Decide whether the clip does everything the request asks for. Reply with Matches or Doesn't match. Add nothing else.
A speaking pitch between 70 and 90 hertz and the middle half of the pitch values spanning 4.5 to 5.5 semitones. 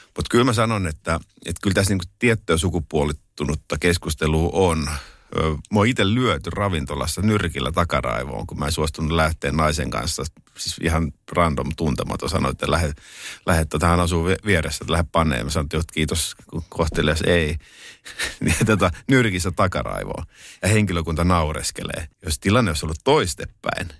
Doesn't match